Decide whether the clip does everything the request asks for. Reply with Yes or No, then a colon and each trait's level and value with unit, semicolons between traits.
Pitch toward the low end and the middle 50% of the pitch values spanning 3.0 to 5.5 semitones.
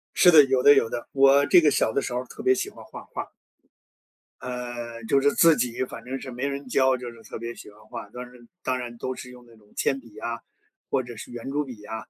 No: low, 125 Hz; narrow, 2.5 semitones